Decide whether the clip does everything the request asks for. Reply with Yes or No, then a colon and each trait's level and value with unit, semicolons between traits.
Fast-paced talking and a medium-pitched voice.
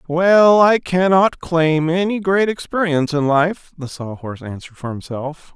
No: average, 160 wpm; medium, 165 Hz